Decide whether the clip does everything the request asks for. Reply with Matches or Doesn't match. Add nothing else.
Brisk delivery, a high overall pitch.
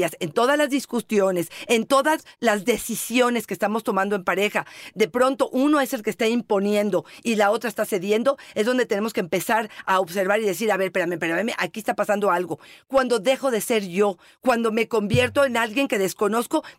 Matches